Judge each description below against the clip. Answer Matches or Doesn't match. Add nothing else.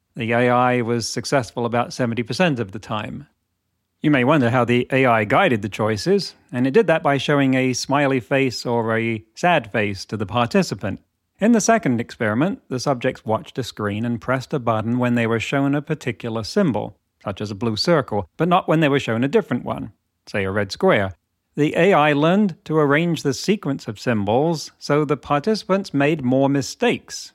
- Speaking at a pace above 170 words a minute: Matches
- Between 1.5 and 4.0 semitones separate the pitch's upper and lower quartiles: Doesn't match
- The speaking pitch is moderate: Doesn't match